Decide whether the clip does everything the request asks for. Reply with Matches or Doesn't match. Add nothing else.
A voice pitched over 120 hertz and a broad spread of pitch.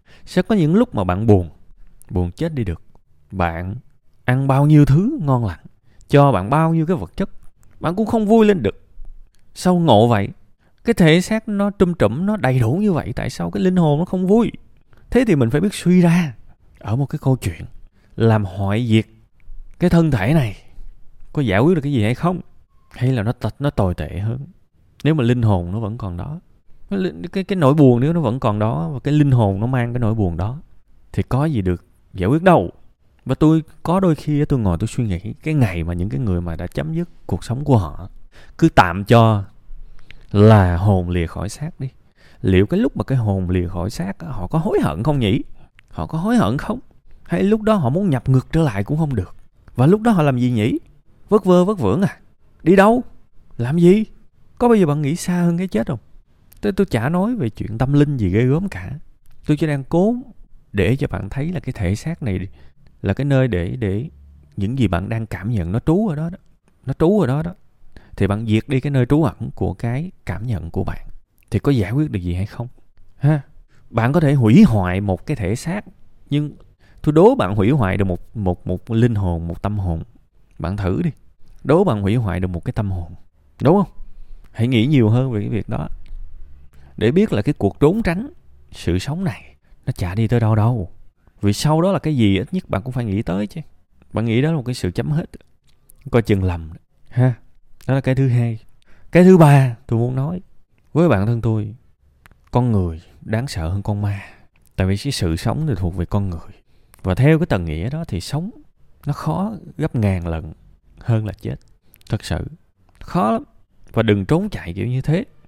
Doesn't match